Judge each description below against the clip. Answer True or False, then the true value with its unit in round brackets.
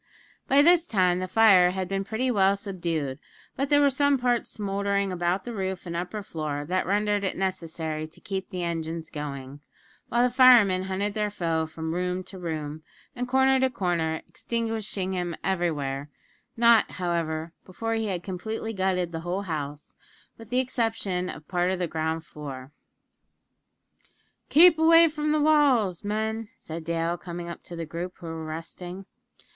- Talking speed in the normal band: True (170 wpm)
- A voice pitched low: False (185 Hz)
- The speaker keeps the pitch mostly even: False (5.0 semitones)